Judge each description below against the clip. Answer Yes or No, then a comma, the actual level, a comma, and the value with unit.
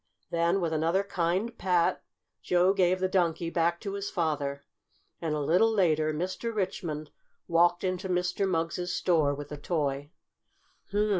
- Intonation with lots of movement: No, average, 2.9 semitones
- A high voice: No, medium, 175 Hz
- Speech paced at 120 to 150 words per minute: Yes, average, 145 wpm